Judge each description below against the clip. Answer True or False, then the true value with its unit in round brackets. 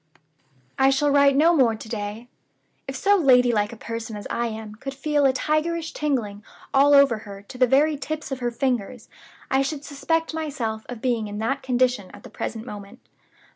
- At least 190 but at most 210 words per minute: True (195 wpm)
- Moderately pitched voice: False (255 Hz)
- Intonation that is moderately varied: True (4.2 semitones)